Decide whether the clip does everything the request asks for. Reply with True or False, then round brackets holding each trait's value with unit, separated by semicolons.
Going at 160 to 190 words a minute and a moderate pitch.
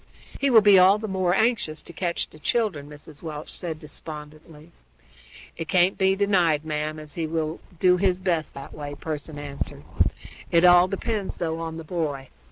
True (175 wpm; 165 Hz)